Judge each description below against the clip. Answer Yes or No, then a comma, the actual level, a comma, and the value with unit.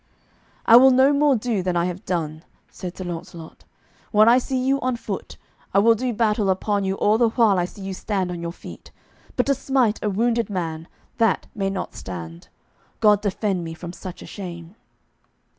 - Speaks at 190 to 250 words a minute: Yes, average, 195 wpm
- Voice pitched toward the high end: Yes, high, 200 Hz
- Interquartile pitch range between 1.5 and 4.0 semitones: No, average, 4.7 semitones